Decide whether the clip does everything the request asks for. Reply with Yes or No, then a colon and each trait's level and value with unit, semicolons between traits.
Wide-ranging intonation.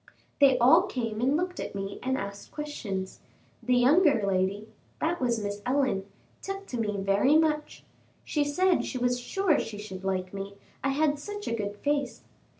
Yes: wide, 6.7 semitones